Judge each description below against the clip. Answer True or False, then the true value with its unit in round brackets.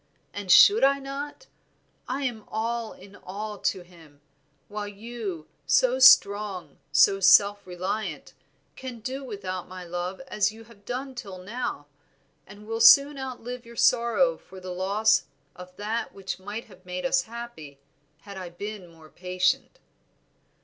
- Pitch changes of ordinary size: True (4.5 semitones)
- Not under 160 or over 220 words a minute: False (150 wpm)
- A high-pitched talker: True (205 Hz)